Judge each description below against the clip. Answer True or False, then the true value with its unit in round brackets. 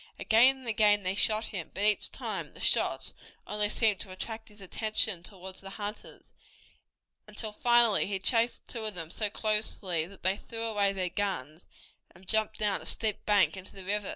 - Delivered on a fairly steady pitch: True (2.3 semitones)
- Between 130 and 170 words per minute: False (185 wpm)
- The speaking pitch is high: True (205 Hz)